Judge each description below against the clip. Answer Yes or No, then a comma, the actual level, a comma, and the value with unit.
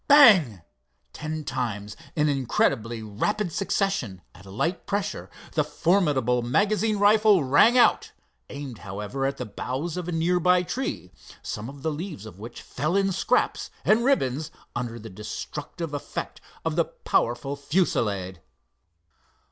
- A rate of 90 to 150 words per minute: Yes, average, 140 wpm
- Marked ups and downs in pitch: Yes, wide, 8.3 semitones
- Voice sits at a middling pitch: Yes, medium, 145 Hz